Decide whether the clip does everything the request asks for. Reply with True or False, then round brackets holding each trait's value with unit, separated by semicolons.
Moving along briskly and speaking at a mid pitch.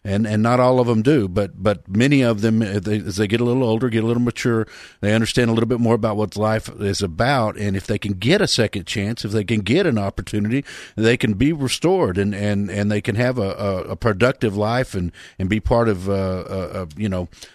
False (245 wpm; 110 Hz)